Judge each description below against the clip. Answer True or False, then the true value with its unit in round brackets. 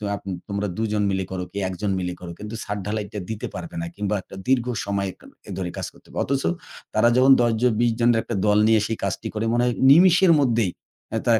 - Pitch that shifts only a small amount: False (3.1 semitones)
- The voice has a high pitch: False (110 Hz)